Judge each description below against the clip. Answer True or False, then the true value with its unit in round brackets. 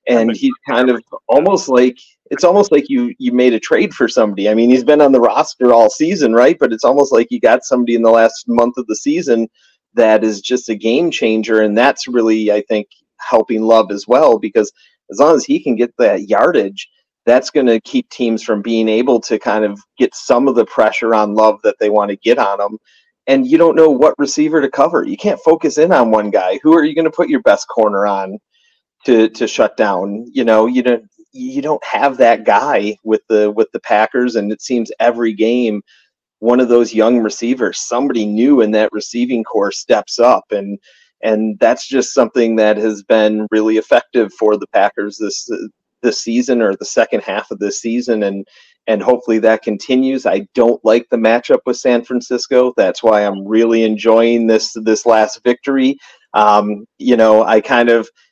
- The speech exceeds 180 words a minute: True (205 wpm)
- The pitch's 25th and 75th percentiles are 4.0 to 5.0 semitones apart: False (2.6 semitones)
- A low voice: True (115 Hz)